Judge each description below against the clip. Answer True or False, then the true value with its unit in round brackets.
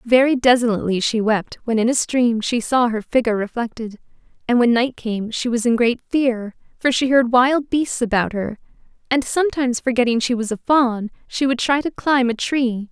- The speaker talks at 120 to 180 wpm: False (200 wpm)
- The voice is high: True (240 Hz)